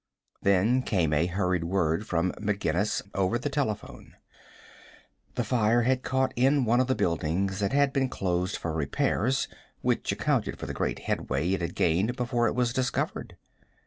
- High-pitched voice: No, low, 105 Hz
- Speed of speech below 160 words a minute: No, average, 165 wpm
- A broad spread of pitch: Yes, wide, 5.9 semitones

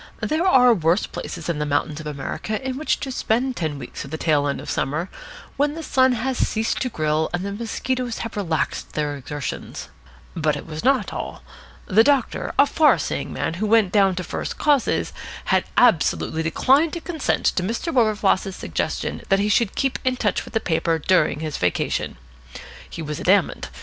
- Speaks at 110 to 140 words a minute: No, average, 190 wpm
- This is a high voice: Yes, high, 200 Hz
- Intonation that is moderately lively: No, wide, 8.3 semitones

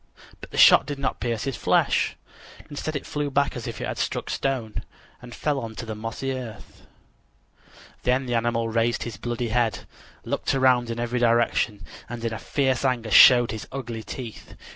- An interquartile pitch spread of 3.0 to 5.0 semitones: No, narrow, 2.4 semitones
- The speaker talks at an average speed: Yes, average, 180 wpm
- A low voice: Yes, low, 120 Hz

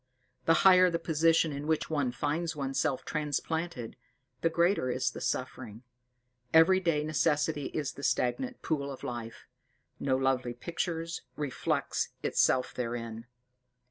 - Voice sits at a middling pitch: Yes, medium, 150 Hz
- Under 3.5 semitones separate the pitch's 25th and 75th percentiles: No, average, 4.3 semitones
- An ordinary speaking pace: No, slow, 125 wpm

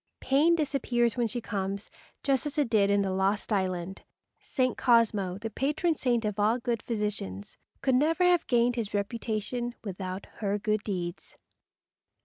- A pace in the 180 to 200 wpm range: No, average, 155 wpm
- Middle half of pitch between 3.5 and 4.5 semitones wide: Yes, average, 4.0 semitones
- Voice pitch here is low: No, high, 225 Hz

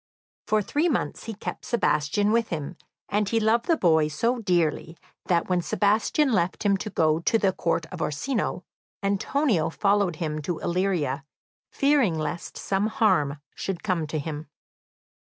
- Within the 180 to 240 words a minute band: No, average, 155 wpm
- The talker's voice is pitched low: No, medium, 185 Hz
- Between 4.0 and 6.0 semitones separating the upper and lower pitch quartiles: Yes, wide, 5.4 semitones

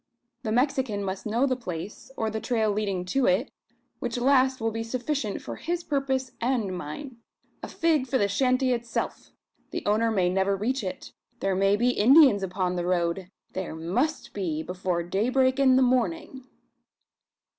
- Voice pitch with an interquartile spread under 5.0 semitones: No, average, 5.3 semitones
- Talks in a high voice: Yes, high, 225 Hz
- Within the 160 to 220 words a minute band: Yes, average, 165 wpm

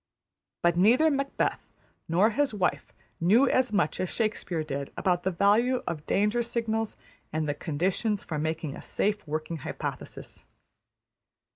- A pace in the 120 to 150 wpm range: Yes, average, 140 wpm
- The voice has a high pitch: Yes, high, 195 Hz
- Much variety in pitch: Yes, wide, 5.9 semitones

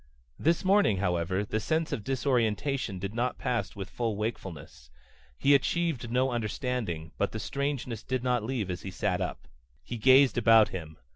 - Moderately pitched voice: No, low, 115 Hz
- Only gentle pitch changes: No, average, 4.8 semitones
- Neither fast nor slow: Yes, average, 165 wpm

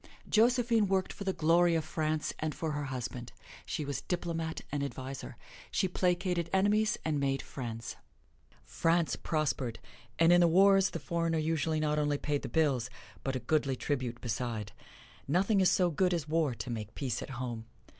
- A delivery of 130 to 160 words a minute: No, average, 175 wpm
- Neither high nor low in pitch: Yes, medium, 155 Hz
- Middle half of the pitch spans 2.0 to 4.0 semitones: No, average, 4.7 semitones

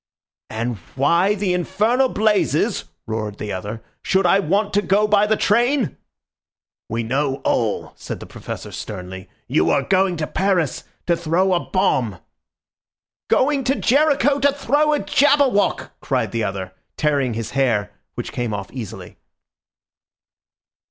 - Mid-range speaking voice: Yes, medium, 180 Hz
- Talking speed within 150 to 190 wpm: No, average, 140 wpm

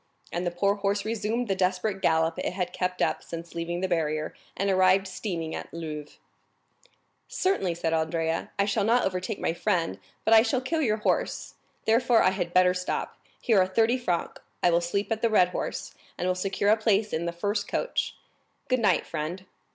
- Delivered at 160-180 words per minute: No, average, 195 wpm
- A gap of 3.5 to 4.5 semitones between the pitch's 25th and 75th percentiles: Yes, average, 3.8 semitones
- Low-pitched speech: No, medium, 185 Hz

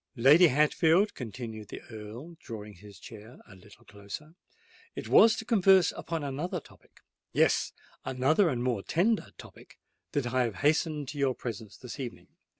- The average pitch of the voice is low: Yes, low, 130 Hz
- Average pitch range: No, wide, 6.3 semitones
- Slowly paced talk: No, average, 155 wpm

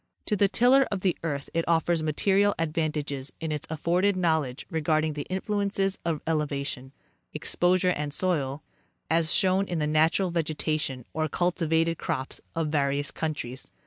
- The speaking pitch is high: No, medium, 160 Hz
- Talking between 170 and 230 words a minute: No, average, 150 wpm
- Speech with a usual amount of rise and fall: Yes, average, 3.4 semitones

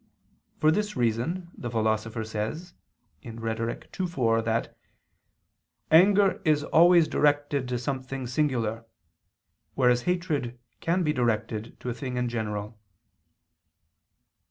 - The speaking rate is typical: No, slow, 110 wpm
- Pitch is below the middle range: Yes, low, 125 Hz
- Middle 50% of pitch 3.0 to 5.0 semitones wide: No, wide, 5.5 semitones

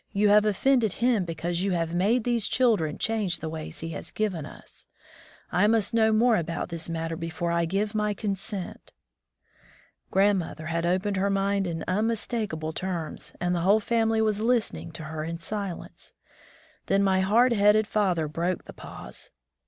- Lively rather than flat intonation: No, average, 4.3 semitones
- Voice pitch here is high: Yes, high, 195 Hz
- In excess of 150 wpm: Yes, average, 170 wpm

